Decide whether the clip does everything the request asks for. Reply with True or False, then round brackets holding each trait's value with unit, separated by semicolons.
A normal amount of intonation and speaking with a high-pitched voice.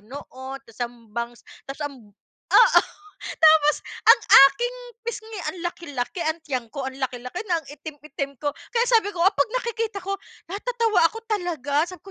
False (6.8 semitones; 315 Hz)